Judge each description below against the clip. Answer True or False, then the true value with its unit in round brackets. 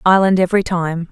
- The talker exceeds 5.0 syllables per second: True (5.9 syllables/s)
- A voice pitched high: False (180 Hz)